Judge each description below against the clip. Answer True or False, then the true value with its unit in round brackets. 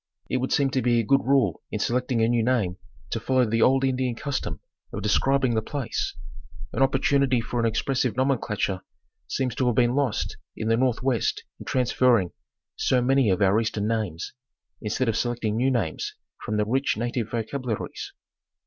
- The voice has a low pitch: True (120 Hz)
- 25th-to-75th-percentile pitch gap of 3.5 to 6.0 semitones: False (2.9 semitones)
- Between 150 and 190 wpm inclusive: True (185 wpm)